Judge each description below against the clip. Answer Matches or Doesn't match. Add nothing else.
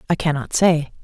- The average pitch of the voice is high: Doesn't match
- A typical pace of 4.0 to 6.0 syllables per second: Matches